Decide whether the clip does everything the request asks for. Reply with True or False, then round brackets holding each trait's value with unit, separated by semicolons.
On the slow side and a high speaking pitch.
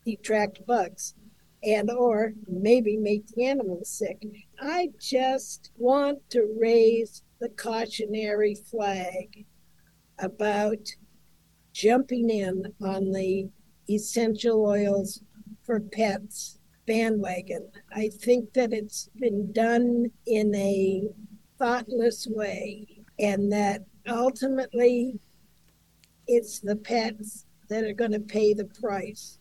True (100 wpm; 215 Hz)